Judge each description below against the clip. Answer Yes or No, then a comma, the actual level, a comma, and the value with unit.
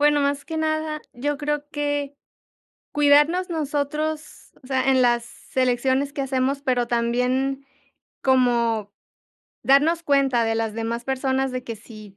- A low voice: No, very high, 270 Hz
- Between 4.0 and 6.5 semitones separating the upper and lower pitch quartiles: No, average, 3.2 semitones